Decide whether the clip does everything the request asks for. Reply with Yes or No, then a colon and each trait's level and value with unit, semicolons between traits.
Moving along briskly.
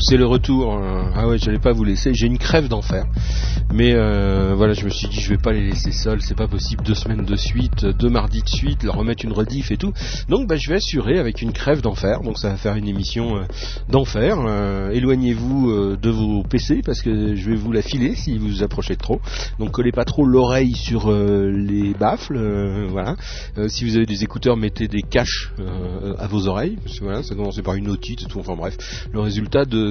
Yes: fast, 235 wpm